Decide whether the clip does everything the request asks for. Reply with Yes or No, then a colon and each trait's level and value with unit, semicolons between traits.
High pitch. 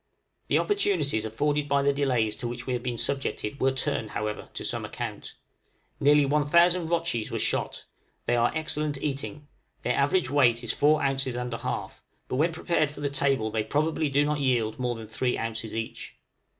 No: medium, 140 Hz